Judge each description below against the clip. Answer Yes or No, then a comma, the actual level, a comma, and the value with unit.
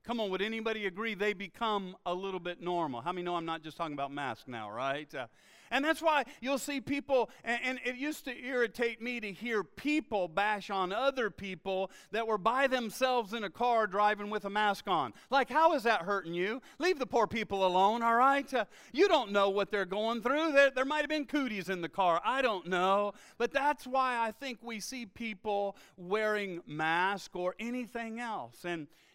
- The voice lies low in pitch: No, high, 220 Hz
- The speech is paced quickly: Yes, fast, 210 wpm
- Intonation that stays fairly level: No, average, 4.7 semitones